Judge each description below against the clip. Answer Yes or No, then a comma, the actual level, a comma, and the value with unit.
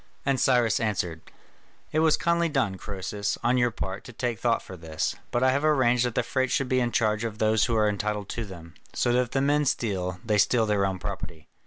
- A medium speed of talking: No, fast, 230 wpm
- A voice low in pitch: Yes, low, 115 Hz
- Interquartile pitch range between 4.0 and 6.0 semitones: Yes, average, 4.3 semitones